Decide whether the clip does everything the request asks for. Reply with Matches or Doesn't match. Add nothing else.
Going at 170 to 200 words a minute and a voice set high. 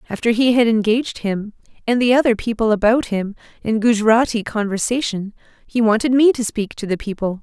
Matches